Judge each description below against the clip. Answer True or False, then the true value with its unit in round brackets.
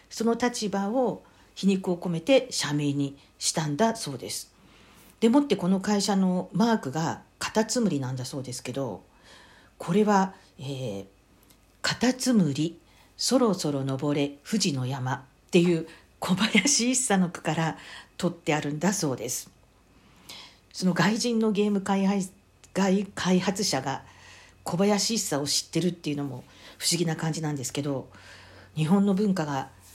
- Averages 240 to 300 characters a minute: True (280 characters per minute)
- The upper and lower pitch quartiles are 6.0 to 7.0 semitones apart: True (6.5 semitones)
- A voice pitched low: False (170 Hz)